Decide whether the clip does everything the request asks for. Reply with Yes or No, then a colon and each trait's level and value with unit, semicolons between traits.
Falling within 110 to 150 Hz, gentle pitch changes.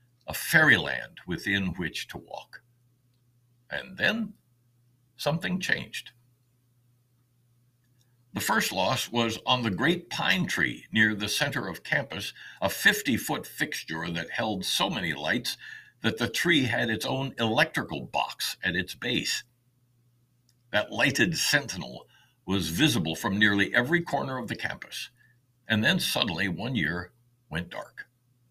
Yes: low, 120 Hz; narrow, 1.2 semitones